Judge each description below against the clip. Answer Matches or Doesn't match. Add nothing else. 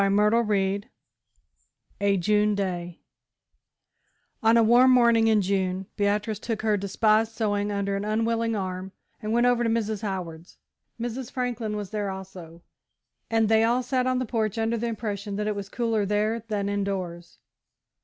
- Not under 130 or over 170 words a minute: Matches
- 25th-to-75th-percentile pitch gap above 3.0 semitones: Doesn't match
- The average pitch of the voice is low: Doesn't match